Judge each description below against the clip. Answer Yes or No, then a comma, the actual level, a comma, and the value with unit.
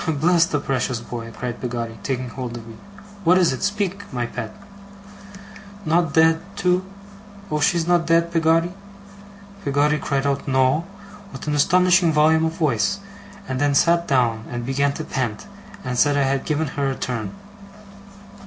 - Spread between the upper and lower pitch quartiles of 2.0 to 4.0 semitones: No, average, 4.5 semitones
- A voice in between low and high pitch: Yes, medium, 145 Hz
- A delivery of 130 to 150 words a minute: No, average, 160 wpm